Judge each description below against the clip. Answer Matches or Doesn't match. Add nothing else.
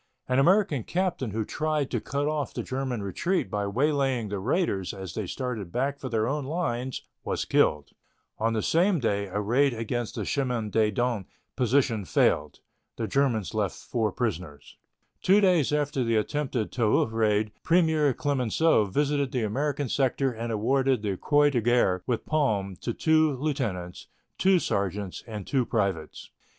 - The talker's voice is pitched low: Matches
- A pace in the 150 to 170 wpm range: Matches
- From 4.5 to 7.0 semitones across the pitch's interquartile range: Matches